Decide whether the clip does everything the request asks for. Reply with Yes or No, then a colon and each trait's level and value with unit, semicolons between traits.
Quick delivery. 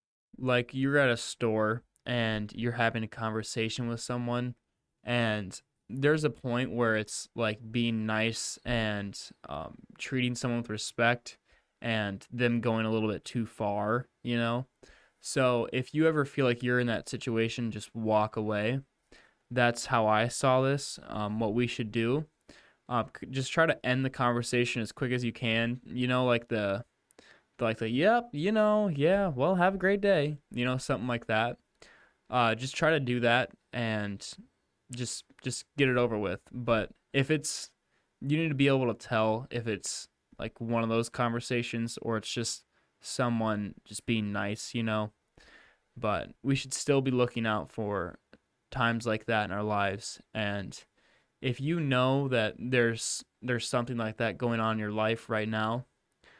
No: average, 170 wpm